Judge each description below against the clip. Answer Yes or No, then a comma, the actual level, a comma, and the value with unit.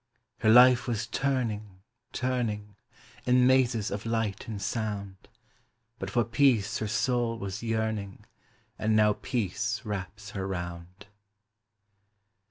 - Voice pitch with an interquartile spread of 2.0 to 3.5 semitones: Yes, average, 3.0 semitones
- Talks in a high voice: No, low, 110 Hz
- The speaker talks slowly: Yes, slow, 115 wpm